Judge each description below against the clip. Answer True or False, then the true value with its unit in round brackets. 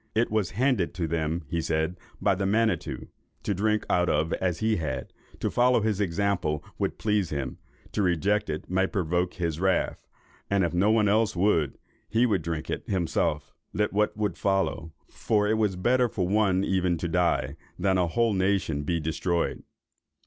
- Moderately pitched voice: False (95 Hz)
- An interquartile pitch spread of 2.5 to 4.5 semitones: True (4.0 semitones)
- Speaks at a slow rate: False (180 wpm)